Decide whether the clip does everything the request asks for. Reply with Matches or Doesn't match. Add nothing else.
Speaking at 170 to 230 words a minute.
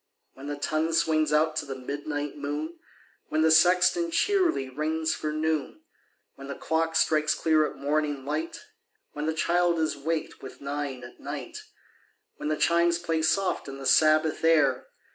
Matches